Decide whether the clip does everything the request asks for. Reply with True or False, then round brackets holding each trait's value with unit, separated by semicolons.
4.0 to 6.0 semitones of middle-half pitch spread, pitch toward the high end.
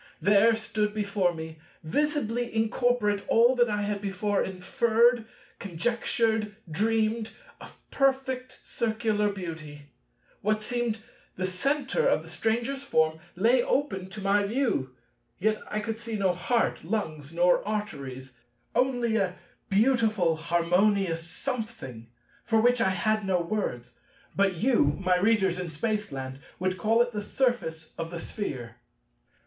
True (4.6 semitones; 210 Hz)